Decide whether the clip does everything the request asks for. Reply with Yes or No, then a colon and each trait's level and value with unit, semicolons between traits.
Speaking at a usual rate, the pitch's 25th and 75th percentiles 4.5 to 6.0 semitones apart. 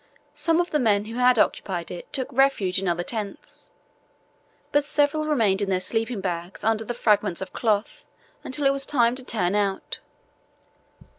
Yes: average, 170 wpm; average, 5.3 semitones